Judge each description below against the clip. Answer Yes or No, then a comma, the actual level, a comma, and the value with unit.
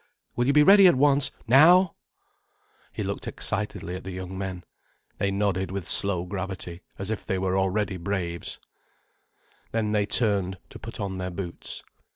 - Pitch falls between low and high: No, very low, 95 Hz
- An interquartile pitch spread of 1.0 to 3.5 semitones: Yes, average, 3.0 semitones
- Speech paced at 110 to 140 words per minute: No, average, 165 wpm